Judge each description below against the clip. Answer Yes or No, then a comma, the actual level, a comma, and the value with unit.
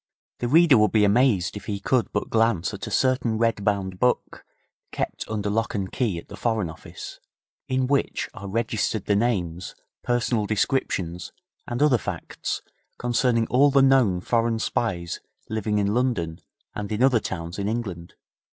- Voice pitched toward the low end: Yes, low, 110 Hz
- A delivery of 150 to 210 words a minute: Yes, average, 165 wpm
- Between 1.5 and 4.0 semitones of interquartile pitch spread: Yes, average, 3.7 semitones